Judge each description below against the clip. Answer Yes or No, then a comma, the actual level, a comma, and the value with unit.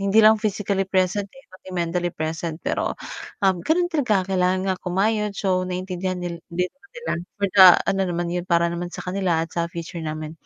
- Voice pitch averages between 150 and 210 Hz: Yes, medium, 185 Hz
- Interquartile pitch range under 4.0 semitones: Yes, average, 2.8 semitones